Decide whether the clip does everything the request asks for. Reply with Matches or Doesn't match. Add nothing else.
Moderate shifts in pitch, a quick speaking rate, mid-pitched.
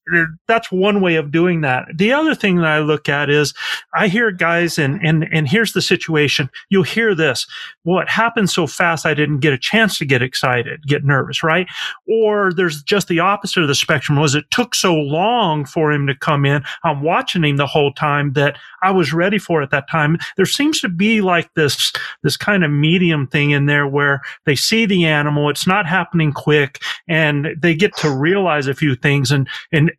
Matches